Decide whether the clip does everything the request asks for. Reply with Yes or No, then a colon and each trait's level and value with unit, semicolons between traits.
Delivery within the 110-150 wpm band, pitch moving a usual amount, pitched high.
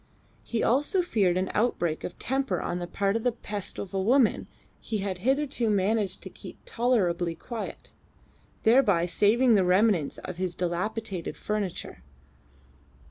Yes: average, 145 wpm; average, 4.5 semitones; high, 205 Hz